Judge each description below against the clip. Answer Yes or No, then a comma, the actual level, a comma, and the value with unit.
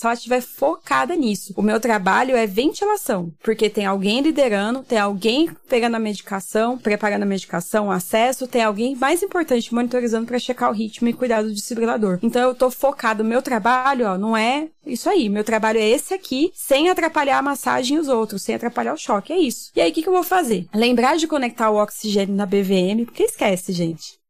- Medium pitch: No, high, 235 Hz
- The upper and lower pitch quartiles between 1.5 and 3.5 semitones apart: No, average, 4.1 semitones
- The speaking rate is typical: No, fast, 205 wpm